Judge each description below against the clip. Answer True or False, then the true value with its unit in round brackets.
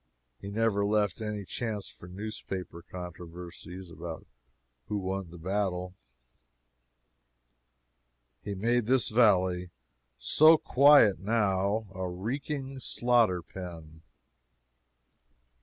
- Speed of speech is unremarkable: False (90 wpm)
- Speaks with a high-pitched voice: False (100 Hz)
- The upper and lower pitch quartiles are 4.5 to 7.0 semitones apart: False (3.9 semitones)